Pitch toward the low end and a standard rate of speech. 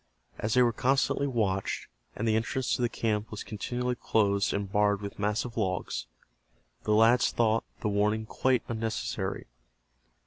Yes: low, 110 Hz; average, 150 wpm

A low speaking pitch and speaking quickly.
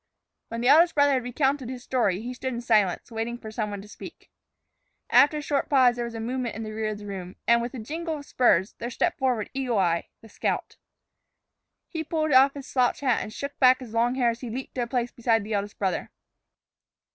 No: high, 240 Hz; fast, 235 wpm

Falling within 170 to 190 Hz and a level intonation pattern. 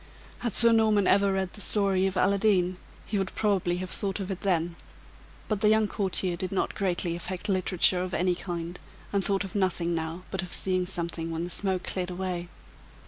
Yes: medium, 185 Hz; narrow, 2.0 semitones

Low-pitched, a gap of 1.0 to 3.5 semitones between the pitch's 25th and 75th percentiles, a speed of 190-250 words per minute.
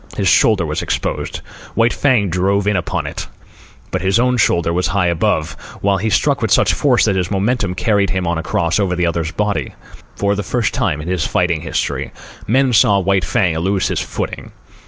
Yes: very low, 95 Hz; average, 3.0 semitones; average, 200 wpm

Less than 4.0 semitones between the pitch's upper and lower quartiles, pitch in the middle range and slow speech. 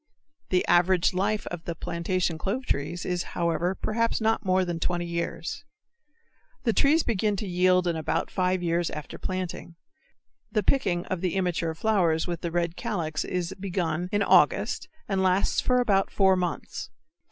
No: narrow, 2.5 semitones; medium, 180 Hz; average, 165 wpm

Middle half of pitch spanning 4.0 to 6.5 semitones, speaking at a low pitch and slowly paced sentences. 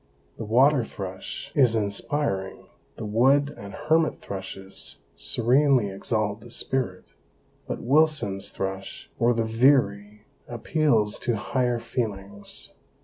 Yes: average, 4.8 semitones; low, 115 Hz; slow, 110 wpm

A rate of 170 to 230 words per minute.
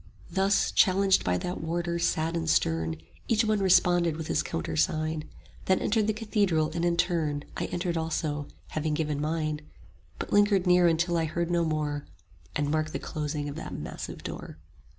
Yes: average, 175 wpm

